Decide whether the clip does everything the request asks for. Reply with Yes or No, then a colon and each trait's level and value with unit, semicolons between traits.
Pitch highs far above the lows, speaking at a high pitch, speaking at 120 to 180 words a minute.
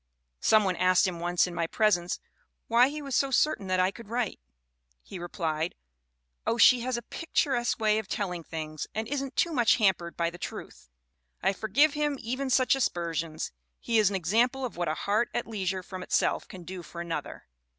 No: wide, 5.7 semitones; high, 200 Hz; average, 195 wpm